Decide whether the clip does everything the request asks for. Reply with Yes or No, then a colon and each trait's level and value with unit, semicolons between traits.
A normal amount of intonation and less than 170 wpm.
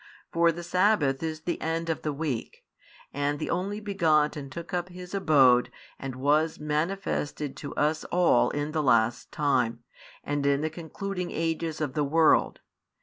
Yes: average, 3.0 semitones; average, 160 wpm